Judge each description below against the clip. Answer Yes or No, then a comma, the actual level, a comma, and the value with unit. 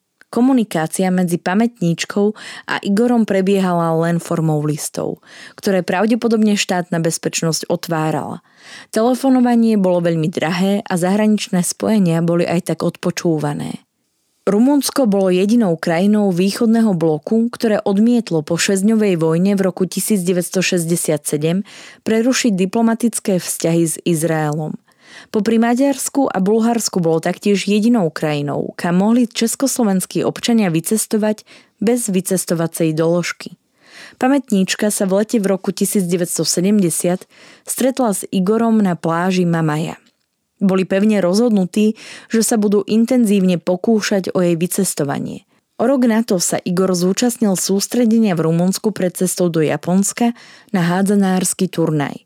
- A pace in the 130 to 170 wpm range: No, average, 115 wpm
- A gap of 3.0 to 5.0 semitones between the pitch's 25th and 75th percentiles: Yes, average, 4.2 semitones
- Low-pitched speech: No, high, 195 Hz